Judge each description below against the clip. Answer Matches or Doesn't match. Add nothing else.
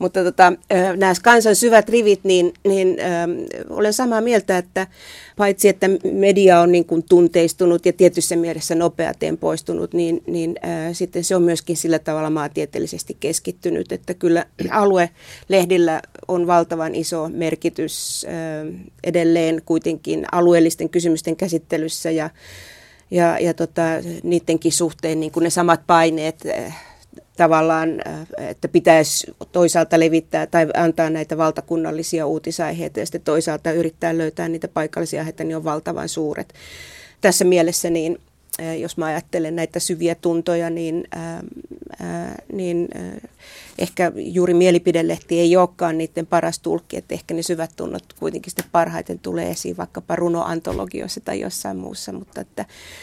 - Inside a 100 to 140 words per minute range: Matches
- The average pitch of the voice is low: Doesn't match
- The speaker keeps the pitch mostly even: Matches